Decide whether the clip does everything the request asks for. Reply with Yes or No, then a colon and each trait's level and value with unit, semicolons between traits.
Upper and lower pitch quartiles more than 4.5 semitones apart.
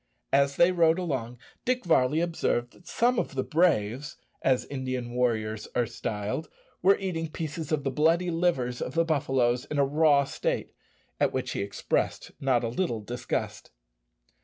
Yes: average, 5.1 semitones